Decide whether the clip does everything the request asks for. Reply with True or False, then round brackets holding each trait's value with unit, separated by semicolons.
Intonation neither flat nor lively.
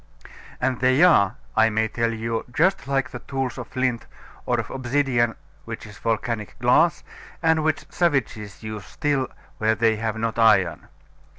True (3.3 semitones)